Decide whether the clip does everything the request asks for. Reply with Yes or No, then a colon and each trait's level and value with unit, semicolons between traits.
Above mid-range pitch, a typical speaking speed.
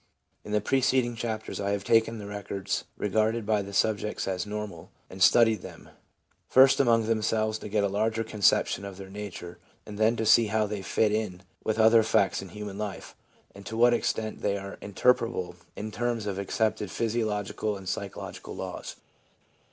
No: low, 105 Hz; average, 175 wpm